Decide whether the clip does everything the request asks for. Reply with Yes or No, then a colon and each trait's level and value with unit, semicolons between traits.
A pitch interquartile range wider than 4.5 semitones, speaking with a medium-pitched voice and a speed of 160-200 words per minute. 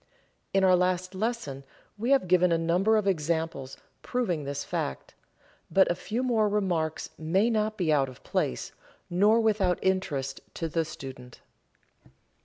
No: average, 5.0 semitones; medium, 180 Hz; average, 150 wpm